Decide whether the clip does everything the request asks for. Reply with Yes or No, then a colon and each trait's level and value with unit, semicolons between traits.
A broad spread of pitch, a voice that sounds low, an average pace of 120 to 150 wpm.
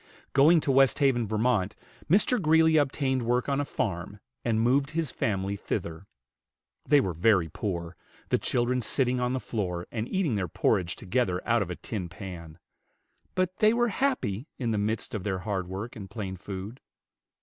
No: wide, 6.3 semitones; low, 115 Hz; average, 170 wpm